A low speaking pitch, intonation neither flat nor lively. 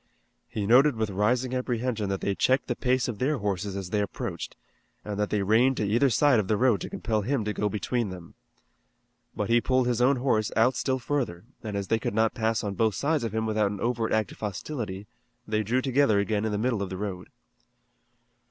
Yes: low, 110 Hz; average, 3.4 semitones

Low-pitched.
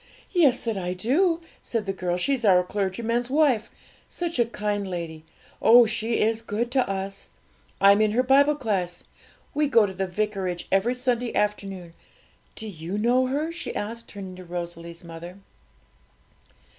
No: high, 210 Hz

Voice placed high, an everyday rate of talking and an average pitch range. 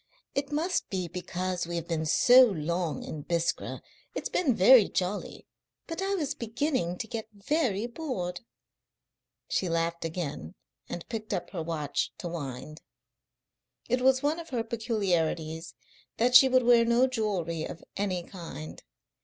No: high, 195 Hz; average, 150 wpm; wide, 6.9 semitones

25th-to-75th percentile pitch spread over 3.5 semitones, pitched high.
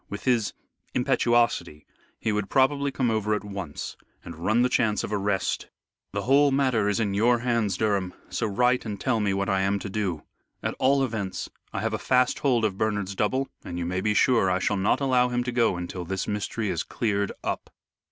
No: average, 3.9 semitones; low, 105 Hz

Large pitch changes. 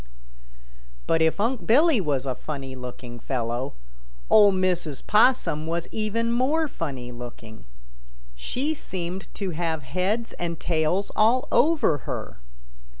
Yes: wide, 8.4 semitones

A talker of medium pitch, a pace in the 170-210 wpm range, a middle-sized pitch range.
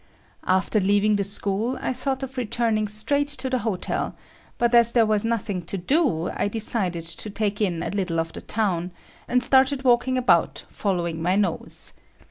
No: high, 215 Hz; average, 175 wpm; average, 4.6 semitones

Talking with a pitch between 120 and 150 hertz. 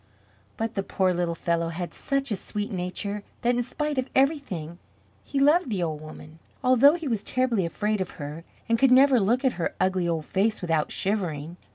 No: high, 205 Hz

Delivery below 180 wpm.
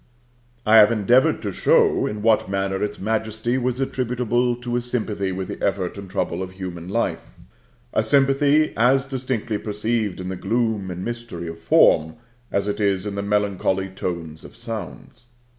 Yes: average, 170 wpm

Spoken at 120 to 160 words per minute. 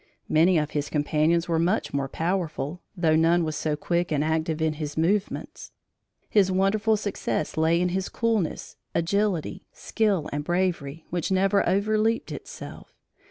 Yes: average, 150 wpm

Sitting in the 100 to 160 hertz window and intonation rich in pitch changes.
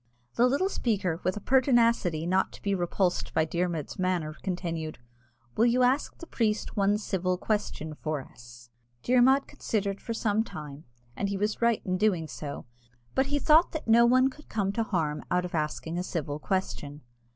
No: high, 190 Hz; wide, 6.3 semitones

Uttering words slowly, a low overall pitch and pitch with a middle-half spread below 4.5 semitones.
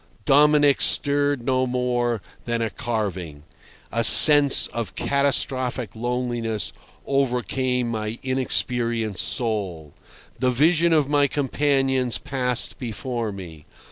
Yes: slow, 105 wpm; low, 125 Hz; average, 3.2 semitones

